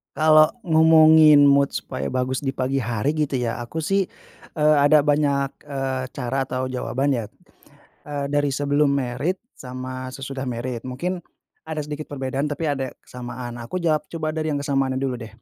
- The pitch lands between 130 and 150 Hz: Yes, medium, 140 Hz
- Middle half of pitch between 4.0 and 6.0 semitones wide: No, average, 2.9 semitones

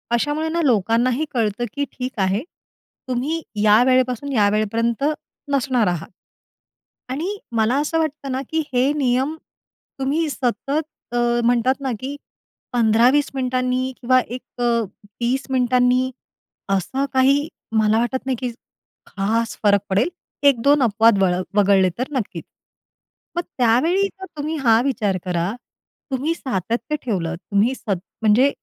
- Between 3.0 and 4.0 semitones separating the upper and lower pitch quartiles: Yes, average, 3.7 semitones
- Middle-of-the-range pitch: No, very high, 250 Hz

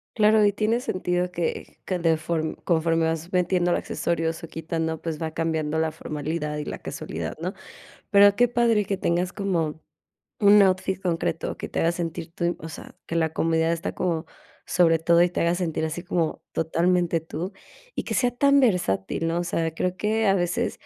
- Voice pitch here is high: No, medium, 170 Hz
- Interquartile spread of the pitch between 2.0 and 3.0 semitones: Yes, narrow, 2.4 semitones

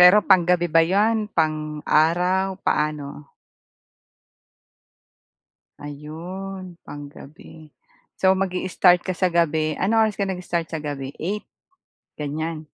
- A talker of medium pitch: Yes, medium, 170 Hz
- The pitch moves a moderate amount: Yes, average, 3.6 semitones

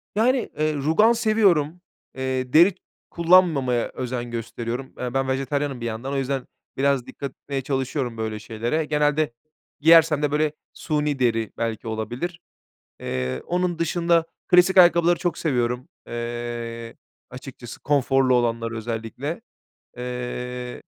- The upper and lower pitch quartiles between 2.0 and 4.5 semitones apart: No, average, 4.9 semitones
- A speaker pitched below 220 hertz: Yes, low, 135 Hz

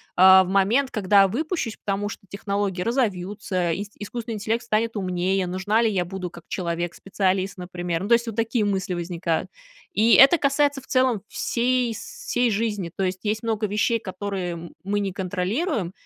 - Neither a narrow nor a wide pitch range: Yes, average, 3.7 semitones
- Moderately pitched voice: No, high, 200 Hz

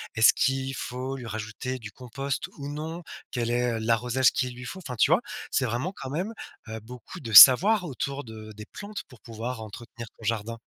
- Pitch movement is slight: No, average, 3.2 semitones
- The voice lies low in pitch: Yes, low, 125 Hz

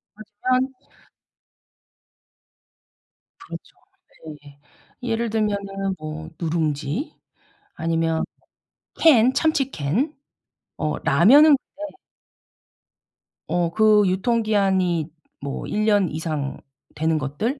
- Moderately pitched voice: No, high, 195 Hz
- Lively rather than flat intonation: Yes, wide, 6.5 semitones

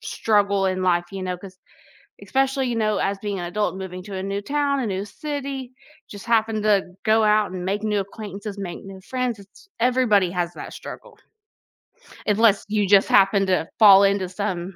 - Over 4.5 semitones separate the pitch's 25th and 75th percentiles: No, average, 2.7 semitones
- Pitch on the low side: No, high, 200 Hz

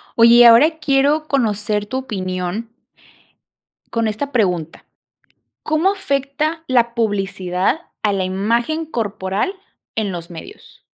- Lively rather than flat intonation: Yes, wide, 6.1 semitones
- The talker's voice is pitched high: Yes, high, 230 Hz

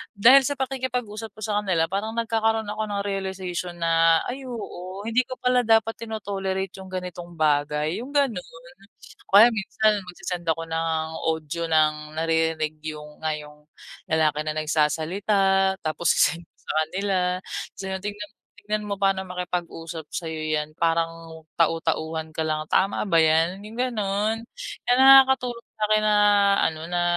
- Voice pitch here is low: No, medium, 185 Hz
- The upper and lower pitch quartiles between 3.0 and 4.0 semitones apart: No, average, 4.8 semitones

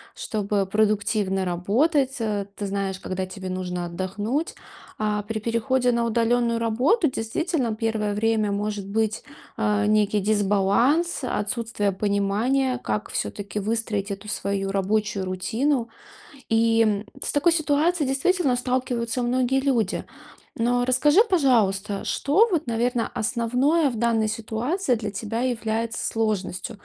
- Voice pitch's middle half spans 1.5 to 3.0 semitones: No, average, 3.6 semitones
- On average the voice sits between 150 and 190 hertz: No, high, 225 Hz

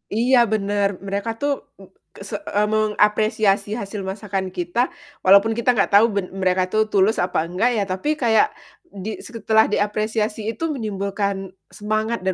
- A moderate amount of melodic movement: No, narrow, 1.9 semitones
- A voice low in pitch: No, high, 210 Hz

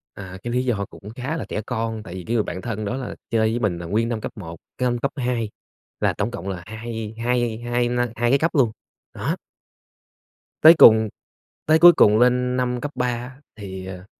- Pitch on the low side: Yes, low, 120 Hz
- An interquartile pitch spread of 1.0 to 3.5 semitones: Yes, average, 2.8 semitones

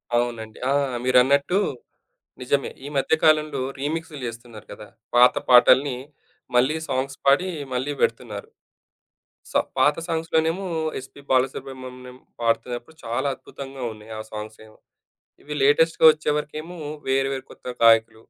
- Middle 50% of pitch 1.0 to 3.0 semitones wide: No, average, 3.5 semitones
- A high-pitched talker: No, low, 130 Hz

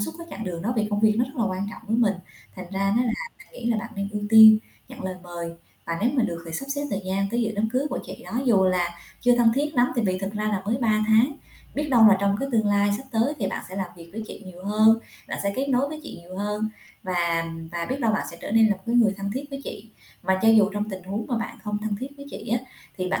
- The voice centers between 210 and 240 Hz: Yes, high, 215 Hz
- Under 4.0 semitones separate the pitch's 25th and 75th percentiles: Yes, average, 3.5 semitones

